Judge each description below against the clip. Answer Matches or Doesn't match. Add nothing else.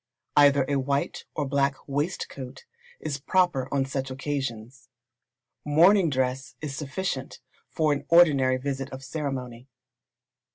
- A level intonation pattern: Matches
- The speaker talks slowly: Matches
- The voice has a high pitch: Doesn't match